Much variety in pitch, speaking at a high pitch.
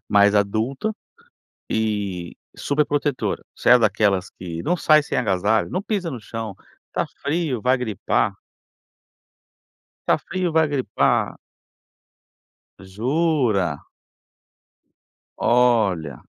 No: wide, 6.4 semitones; low, 115 Hz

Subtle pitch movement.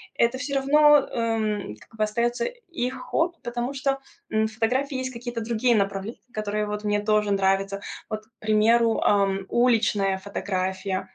No: average, 3.2 semitones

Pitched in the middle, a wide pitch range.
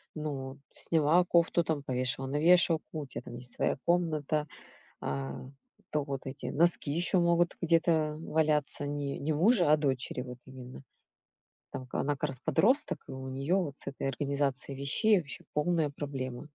No: medium, 145 Hz; average, 3.6 semitones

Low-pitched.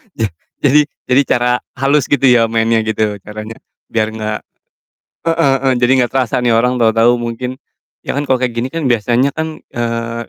Yes: low, 120 Hz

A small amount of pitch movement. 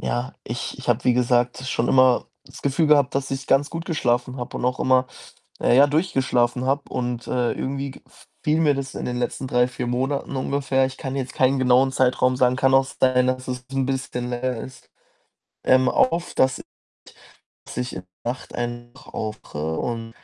Yes: narrow, 1.6 semitones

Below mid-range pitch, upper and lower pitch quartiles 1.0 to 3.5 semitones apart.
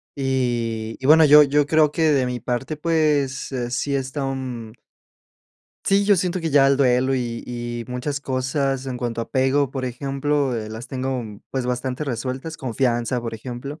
Yes: low, 130 Hz; average, 2.7 semitones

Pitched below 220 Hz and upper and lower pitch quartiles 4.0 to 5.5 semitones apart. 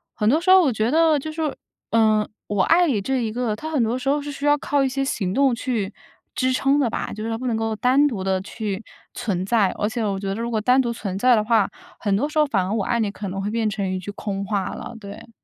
No: high, 230 Hz; average, 4.6 semitones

